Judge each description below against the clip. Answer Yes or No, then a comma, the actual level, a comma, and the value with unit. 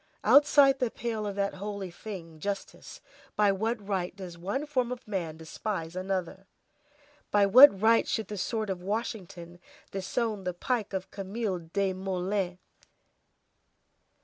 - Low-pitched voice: No, high, 200 Hz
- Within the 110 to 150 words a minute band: Yes, slow, 135 wpm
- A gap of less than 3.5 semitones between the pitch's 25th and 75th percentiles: Yes, average, 3.1 semitones